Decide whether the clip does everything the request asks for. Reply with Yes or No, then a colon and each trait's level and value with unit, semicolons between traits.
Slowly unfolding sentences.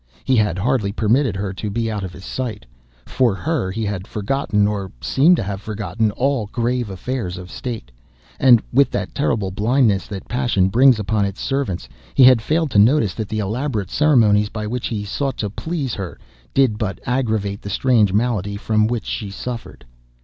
No: average, 190 wpm